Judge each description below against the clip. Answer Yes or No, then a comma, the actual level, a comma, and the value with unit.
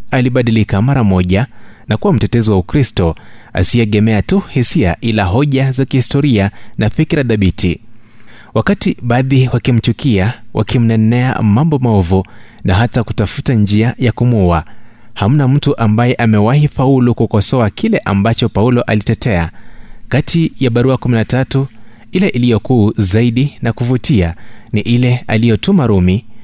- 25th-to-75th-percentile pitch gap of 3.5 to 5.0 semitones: No, average, 3.1 semitones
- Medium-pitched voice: No, low, 115 Hz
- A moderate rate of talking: Yes, average, 120 wpm